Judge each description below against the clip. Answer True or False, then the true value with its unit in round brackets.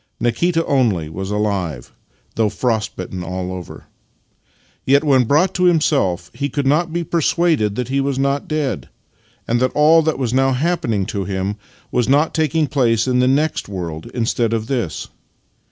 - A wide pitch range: True (6.5 semitones)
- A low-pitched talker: True (125 Hz)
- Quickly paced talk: False (170 wpm)